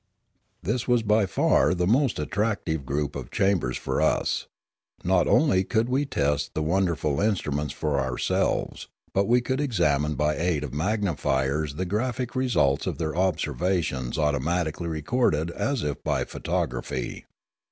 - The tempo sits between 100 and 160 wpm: Yes, average, 145 wpm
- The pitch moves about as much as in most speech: No, wide, 6.4 semitones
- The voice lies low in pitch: Yes, very low, 85 Hz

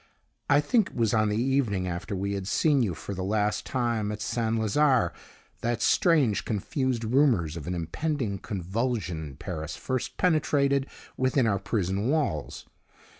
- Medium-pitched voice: No, low, 110 Hz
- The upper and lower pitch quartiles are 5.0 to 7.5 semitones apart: Yes, wide, 5.5 semitones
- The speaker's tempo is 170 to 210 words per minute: No, average, 160 wpm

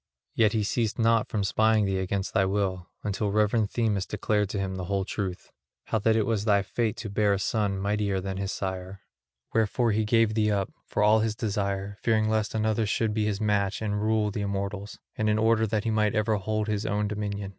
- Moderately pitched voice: No, low, 105 Hz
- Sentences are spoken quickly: Yes, fast, 220 wpm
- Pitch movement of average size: No, narrow, 1.7 semitones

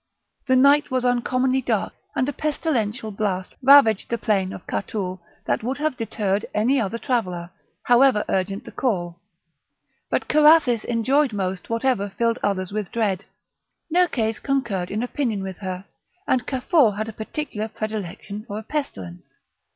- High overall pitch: Yes, high, 225 Hz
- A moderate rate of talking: Yes, average, 150 wpm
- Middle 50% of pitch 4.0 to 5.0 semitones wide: Yes, average, 4.6 semitones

